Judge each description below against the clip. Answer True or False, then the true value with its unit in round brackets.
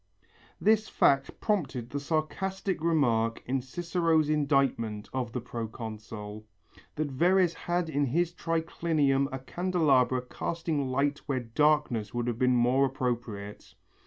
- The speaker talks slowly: True (125 wpm)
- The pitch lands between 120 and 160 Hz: True (135 Hz)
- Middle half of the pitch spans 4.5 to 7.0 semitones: True (5.1 semitones)